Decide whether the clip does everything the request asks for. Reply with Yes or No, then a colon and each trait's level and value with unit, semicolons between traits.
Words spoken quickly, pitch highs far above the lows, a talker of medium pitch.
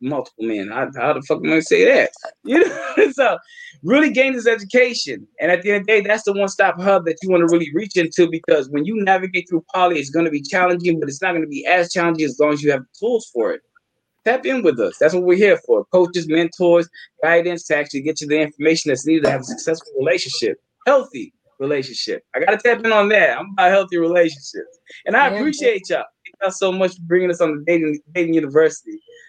Yes: fast, 230 wpm; wide, 8.2 semitones; medium, 180 Hz